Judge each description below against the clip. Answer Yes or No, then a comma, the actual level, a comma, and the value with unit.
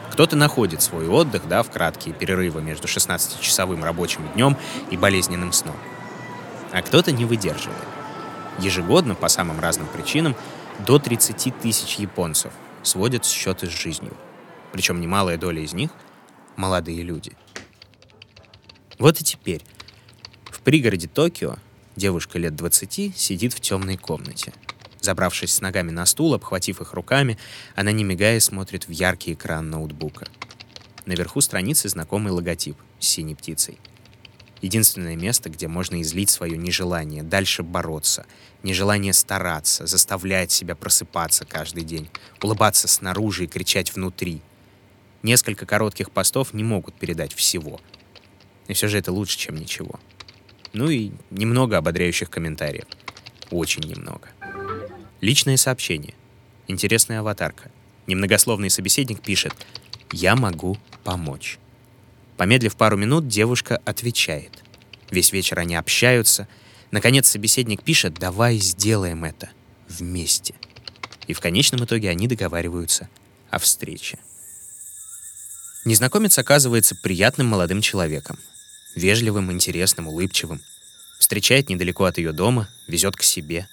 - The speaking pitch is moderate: No, low, 100 Hz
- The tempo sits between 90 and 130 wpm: Yes, average, 120 wpm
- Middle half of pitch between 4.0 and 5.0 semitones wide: Yes, average, 4.4 semitones